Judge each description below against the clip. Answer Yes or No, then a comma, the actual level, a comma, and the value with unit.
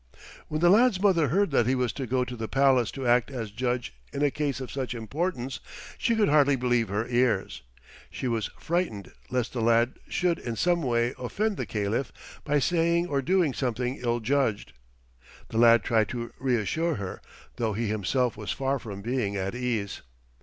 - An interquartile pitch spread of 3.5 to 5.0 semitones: Yes, average, 3.9 semitones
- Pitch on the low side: Yes, low, 125 Hz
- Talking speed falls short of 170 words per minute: No, average, 190 wpm